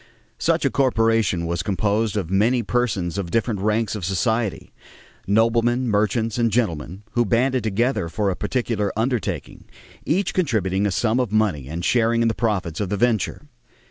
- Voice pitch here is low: Yes, low, 110 Hz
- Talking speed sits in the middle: Yes, average, 165 wpm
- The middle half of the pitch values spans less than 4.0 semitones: Yes, average, 3.4 semitones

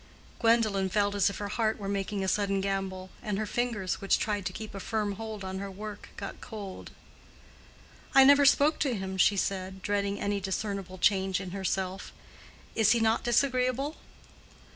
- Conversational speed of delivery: Yes, average, 175 wpm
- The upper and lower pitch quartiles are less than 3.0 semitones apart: Yes, narrow, 2.4 semitones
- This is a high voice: Yes, high, 200 Hz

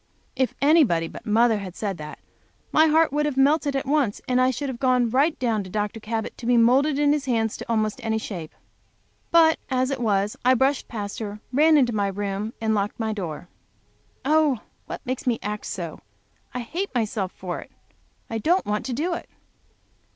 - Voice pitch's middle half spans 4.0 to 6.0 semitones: Yes, average, 5.0 semitones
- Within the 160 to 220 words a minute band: Yes, average, 195 wpm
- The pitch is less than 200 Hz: No, high, 235 Hz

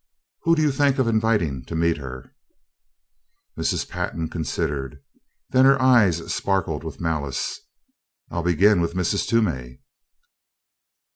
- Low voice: Yes, very low, 85 Hz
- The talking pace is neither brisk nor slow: No, slow, 125 wpm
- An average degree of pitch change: No, wide, 6.8 semitones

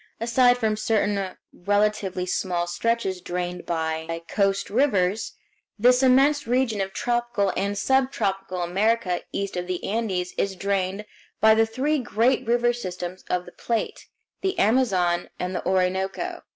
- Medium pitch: No, high, 200 Hz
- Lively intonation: No, average, 4.3 semitones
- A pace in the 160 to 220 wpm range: No, average, 140 wpm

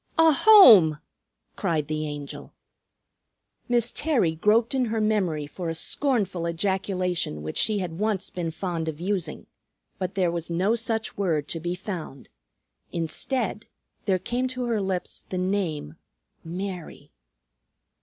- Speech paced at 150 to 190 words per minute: No, slow, 135 wpm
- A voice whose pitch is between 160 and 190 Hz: Yes, medium, 185 Hz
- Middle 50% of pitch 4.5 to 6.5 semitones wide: Yes, average, 4.9 semitones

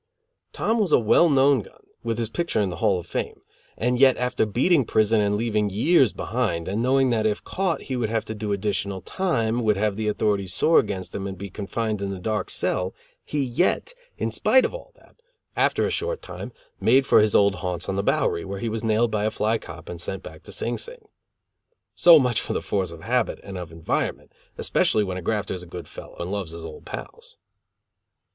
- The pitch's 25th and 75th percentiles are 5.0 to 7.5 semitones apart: No, average, 4.3 semitones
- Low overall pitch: Yes, low, 110 Hz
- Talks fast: Yes, fast, 220 wpm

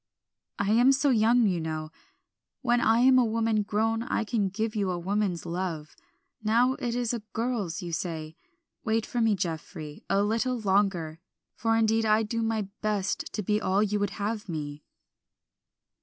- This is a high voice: Yes, high, 215 Hz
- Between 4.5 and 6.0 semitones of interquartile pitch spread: No, average, 3.6 semitones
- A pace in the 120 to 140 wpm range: No, average, 170 wpm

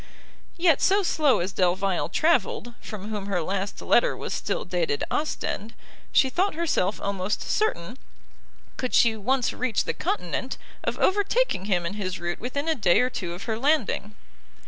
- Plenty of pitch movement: Yes, wide, 8.2 semitones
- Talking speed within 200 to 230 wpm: No, average, 165 wpm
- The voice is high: Yes, high, 220 Hz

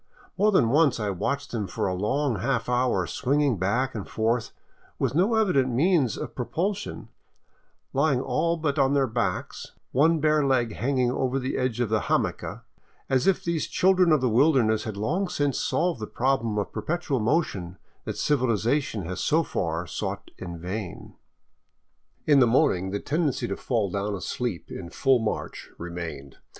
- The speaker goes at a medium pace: Yes, average, 170 wpm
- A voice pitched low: Yes, low, 125 Hz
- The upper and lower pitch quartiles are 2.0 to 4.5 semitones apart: No, wide, 5.6 semitones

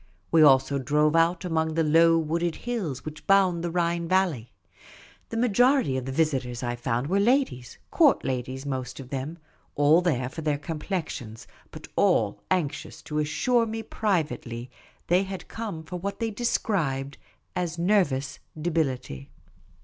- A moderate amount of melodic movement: No, wide, 5.8 semitones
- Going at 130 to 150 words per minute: No, average, 160 wpm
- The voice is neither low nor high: Yes, medium, 160 Hz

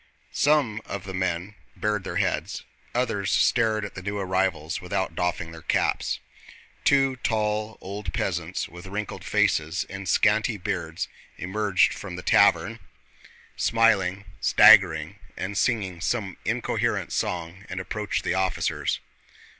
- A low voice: Yes, very low, 95 Hz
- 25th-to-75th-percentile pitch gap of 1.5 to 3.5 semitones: Yes, average, 2.9 semitones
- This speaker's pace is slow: Yes, slow, 130 wpm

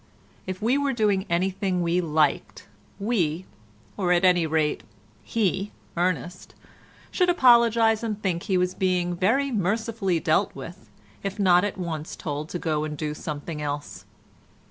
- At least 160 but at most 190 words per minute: No, average, 145 wpm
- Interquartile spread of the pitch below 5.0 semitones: Yes, average, 4.4 semitones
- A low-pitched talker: No, medium, 180 Hz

